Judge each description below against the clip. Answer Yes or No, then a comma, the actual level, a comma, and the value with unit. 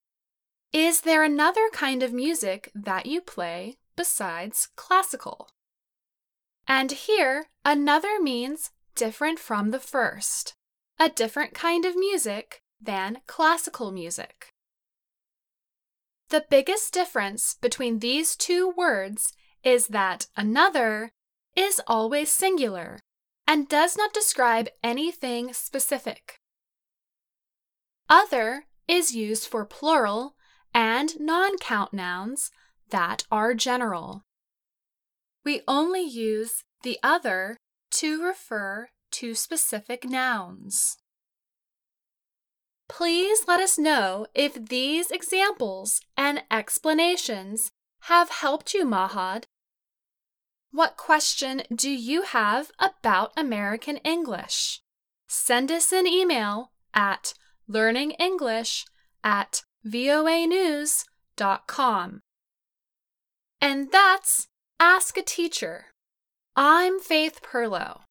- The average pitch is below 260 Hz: No, very high, 280 Hz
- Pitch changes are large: Yes, wide, 6.5 semitones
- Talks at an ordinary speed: No, slow, 90 wpm